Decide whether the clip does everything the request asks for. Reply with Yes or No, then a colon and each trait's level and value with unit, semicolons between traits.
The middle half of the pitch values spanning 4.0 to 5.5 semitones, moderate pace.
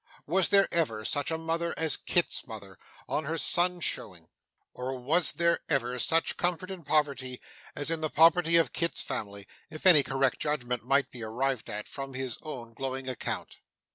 Yes: average, 4.7 semitones; average, 175 wpm